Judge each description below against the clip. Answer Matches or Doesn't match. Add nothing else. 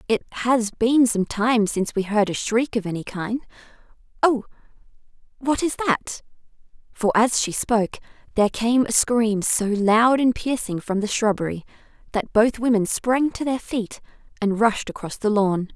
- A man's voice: Doesn't match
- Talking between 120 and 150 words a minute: Doesn't match